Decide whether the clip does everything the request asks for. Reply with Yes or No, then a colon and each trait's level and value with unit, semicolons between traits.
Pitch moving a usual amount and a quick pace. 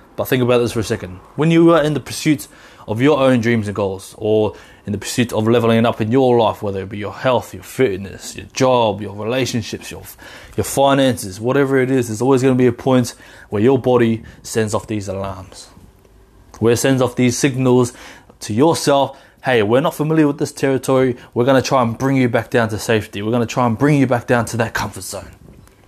Yes: average, 3.6 semitones; fast, 230 wpm